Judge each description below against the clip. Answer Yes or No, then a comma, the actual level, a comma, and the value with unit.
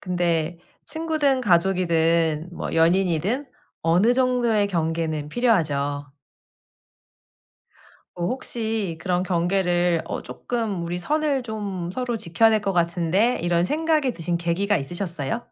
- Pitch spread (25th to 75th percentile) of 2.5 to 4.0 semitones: No, average, 5.2 semitones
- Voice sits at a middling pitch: Yes, medium, 180 Hz